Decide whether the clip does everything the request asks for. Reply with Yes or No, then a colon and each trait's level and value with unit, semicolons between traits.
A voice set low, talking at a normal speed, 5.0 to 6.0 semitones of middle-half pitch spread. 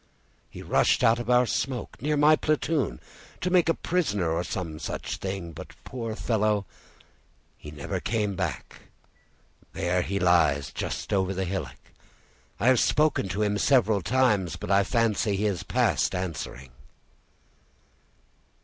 Yes: low, 100 Hz; average, 145 wpm; wide, 5.5 semitones